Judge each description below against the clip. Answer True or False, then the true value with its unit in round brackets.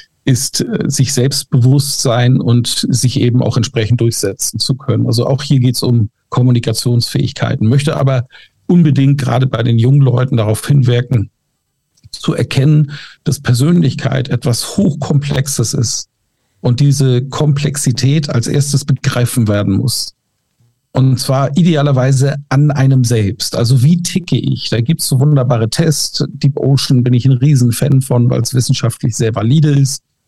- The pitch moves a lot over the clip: False (2.6 semitones)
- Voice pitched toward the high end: False (130 Hz)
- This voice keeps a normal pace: True (145 wpm)